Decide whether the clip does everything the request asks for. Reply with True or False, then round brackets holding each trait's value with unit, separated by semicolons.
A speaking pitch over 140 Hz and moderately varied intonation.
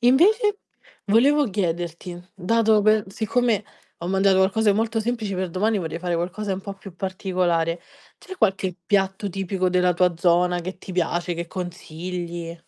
True (190 Hz; 3.3 semitones)